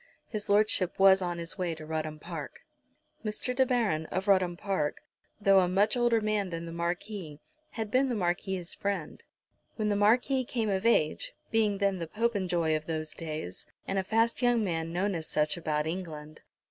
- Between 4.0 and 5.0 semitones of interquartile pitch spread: Yes, average, 4.4 semitones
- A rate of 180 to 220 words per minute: Yes, average, 185 wpm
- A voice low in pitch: No, high, 190 Hz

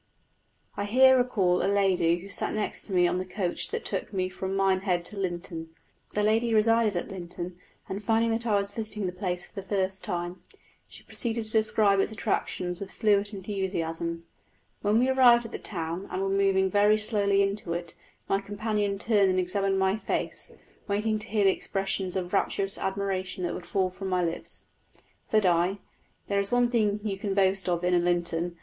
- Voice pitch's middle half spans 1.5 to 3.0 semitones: Yes, narrow, 2.6 semitones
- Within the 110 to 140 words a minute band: No, average, 195 wpm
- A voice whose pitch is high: Yes, high, 195 Hz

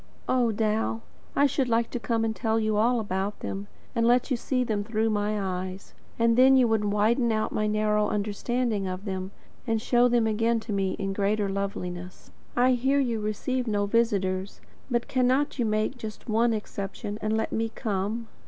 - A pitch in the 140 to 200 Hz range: No, high, 220 Hz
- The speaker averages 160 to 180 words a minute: No, average, 190 wpm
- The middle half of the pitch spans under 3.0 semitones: Yes, narrow, 2.6 semitones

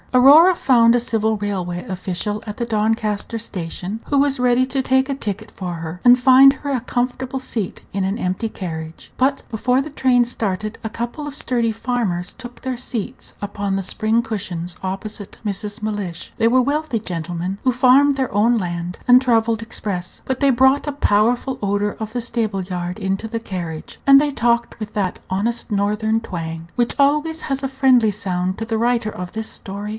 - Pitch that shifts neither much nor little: Yes, average, 4.5 semitones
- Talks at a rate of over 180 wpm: Yes, average, 190 wpm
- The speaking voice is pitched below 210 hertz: No, high, 225 Hz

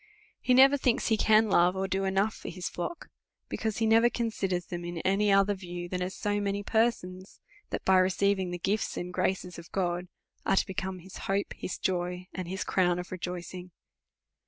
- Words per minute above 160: Yes, average, 195 wpm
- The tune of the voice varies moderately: No, narrow, 2.3 semitones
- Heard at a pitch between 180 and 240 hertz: Yes, high, 190 Hz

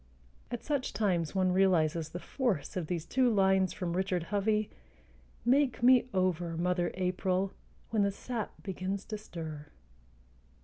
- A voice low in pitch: No, high, 190 Hz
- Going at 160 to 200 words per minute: No, average, 140 wpm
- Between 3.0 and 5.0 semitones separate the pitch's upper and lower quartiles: Yes, average, 3.4 semitones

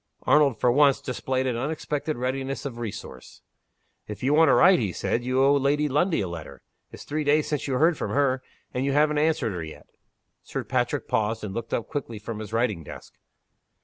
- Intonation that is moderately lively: Yes, average, 4.4 semitones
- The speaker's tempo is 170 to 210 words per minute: Yes, fast, 205 wpm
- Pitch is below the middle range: Yes, low, 130 Hz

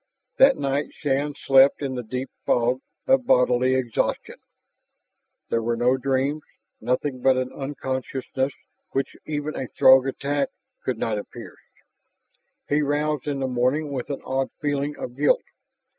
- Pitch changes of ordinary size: No, narrow, 2.2 semitones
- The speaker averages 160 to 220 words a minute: No, average, 145 wpm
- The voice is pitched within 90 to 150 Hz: Yes, low, 135 Hz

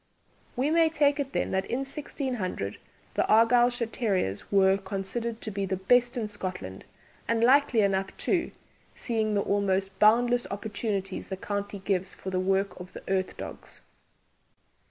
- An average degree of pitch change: Yes, average, 4.1 semitones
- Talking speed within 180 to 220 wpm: No, average, 155 wpm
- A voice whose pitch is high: Yes, high, 205 Hz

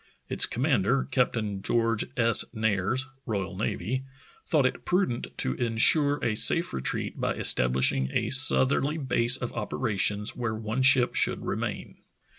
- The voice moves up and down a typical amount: Yes, average, 4.0 semitones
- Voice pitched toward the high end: No, low, 115 Hz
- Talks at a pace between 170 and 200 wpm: No, slow, 135 wpm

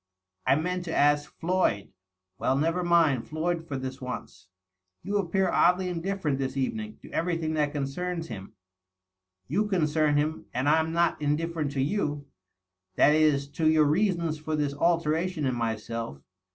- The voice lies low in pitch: No, medium, 155 Hz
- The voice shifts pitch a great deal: No, average, 3.8 semitones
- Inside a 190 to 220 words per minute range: No, average, 165 wpm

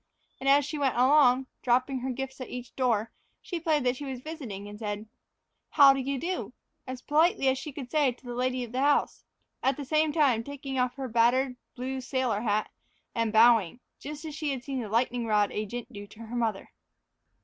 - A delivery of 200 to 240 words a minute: Yes, fast, 205 wpm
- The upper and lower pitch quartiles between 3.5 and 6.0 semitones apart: No, average, 2.9 semitones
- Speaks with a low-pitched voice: No, very high, 255 Hz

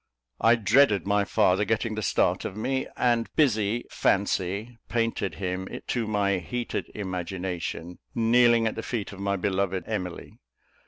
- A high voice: No, low, 105 Hz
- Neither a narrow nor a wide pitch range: Yes, average, 3.4 semitones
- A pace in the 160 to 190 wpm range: No, average, 145 wpm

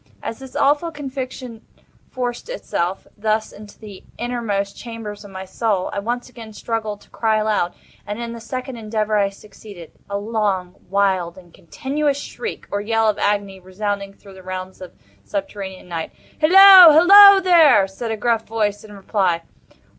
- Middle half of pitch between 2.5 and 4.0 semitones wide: Yes, average, 3.6 semitones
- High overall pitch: Yes, high, 215 Hz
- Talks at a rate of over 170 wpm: No, average, 165 wpm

